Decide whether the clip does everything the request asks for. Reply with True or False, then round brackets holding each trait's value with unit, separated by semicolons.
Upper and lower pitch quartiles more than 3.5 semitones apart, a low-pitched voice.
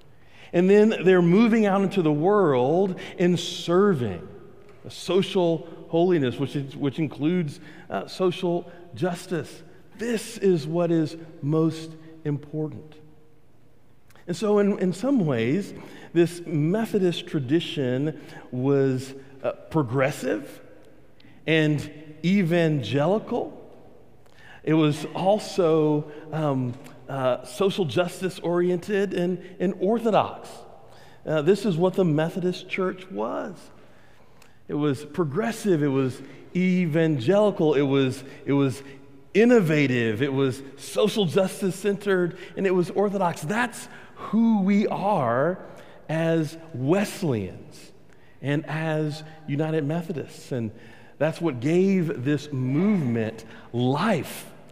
False (4.6 semitones; 160 Hz)